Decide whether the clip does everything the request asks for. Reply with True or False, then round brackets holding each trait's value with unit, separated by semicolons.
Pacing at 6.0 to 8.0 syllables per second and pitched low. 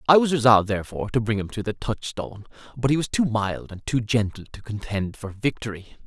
True (6.1 syllables/s; 110 Hz)